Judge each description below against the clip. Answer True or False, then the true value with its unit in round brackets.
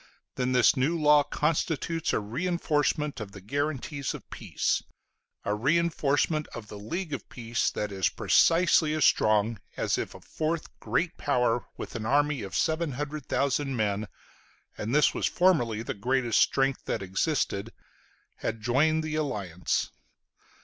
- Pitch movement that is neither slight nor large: False (5.7 semitones)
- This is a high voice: False (135 Hz)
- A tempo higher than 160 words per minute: False (140 wpm)